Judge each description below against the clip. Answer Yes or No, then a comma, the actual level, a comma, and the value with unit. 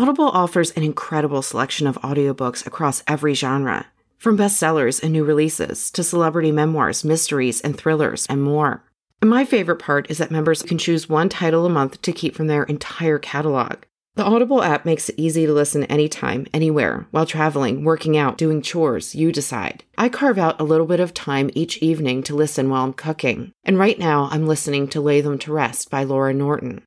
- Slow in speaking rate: No, average, 195 wpm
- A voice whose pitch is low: No, medium, 155 Hz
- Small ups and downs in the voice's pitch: Yes, narrow, 2.3 semitones